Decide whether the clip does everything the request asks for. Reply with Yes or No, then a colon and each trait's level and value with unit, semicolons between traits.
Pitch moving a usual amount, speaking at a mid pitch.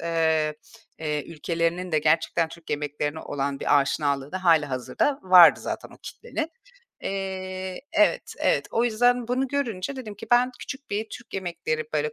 No: wide, 6.5 semitones; medium, 175 Hz